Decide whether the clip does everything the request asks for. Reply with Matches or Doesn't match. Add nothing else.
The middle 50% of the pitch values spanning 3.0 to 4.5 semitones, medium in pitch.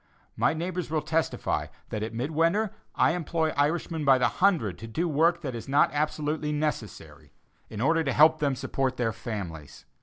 Doesn't match